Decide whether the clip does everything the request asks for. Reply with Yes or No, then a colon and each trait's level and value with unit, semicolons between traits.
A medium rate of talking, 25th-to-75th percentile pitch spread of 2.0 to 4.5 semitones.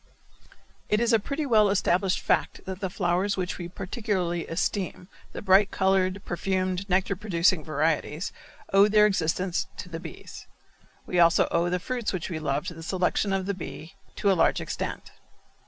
Yes: average, 170 wpm; narrow, 2.5 semitones